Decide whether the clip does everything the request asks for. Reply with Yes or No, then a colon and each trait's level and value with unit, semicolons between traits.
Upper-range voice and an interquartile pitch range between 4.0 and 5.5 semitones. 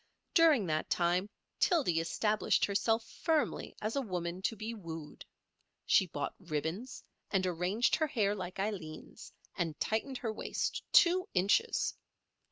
Yes: high, 205 Hz; average, 5.1 semitones